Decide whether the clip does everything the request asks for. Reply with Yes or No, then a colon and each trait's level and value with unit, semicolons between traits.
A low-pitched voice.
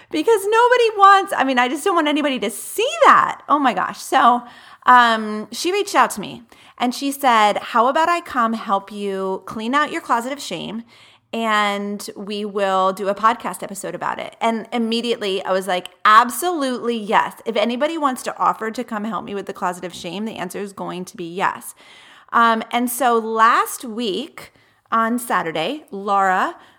No: high, 230 Hz